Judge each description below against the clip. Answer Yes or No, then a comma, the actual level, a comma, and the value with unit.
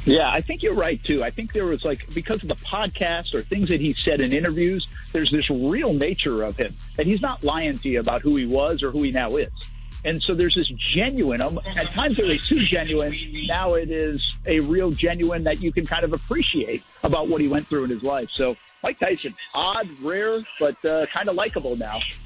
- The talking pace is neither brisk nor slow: No, fast, 230 wpm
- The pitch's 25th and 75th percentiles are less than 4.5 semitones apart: Yes, average, 3.3 semitones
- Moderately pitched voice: Yes, medium, 160 Hz